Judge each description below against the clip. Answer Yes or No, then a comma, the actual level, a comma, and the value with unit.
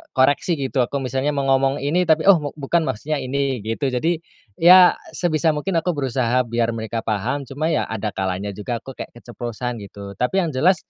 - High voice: No, low, 135 Hz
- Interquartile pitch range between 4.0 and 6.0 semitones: Yes, average, 4.7 semitones